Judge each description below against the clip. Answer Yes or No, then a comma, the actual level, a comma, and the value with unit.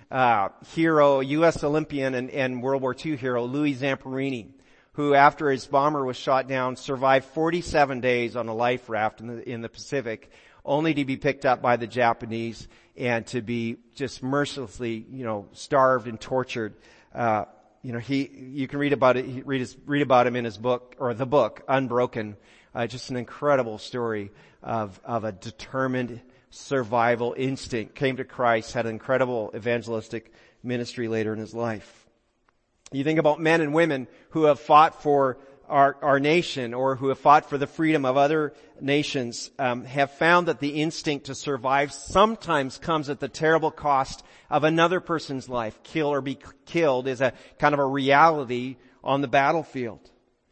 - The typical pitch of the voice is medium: No, low, 130 Hz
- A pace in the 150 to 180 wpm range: Yes, average, 175 wpm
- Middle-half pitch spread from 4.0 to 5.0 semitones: No, average, 3.1 semitones